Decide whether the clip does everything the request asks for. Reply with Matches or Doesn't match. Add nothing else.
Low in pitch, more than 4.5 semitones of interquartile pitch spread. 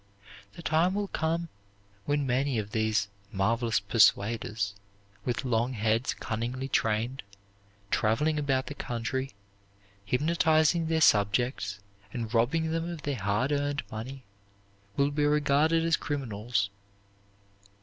Matches